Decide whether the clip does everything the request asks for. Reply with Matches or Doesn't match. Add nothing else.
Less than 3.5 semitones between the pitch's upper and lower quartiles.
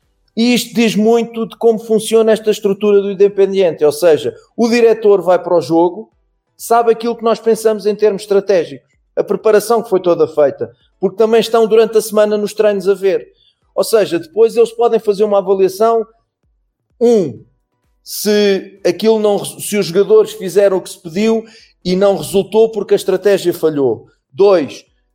Matches